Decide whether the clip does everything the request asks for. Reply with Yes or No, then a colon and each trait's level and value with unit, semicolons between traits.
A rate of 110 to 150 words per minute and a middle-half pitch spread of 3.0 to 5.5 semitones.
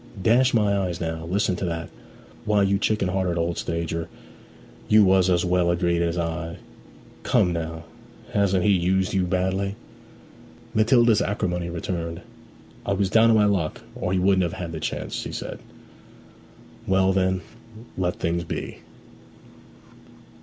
No: average, 145 wpm; narrow, 2.6 semitones